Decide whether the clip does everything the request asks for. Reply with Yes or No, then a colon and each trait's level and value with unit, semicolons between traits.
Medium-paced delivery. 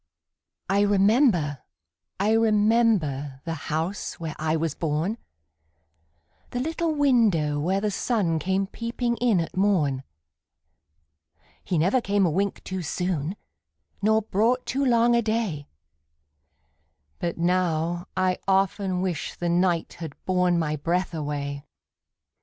No: slow, 125 wpm